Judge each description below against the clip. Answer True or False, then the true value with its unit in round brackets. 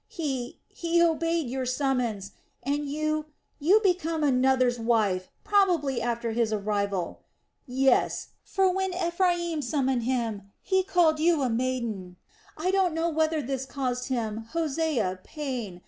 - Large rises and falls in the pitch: True (5.7 semitones)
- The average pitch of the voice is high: True (270 Hz)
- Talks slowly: True (130 wpm)